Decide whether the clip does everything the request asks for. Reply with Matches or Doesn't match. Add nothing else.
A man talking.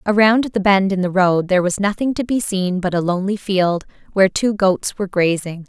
Doesn't match